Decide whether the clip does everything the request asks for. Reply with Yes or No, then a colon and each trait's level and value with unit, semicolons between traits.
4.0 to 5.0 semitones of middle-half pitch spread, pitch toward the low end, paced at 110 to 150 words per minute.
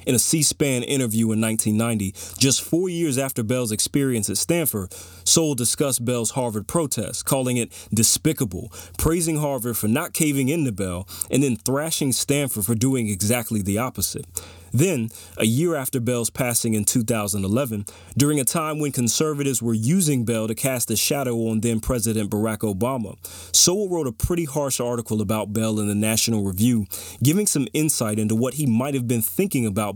No: average, 4.5 semitones; low, 120 Hz; average, 175 wpm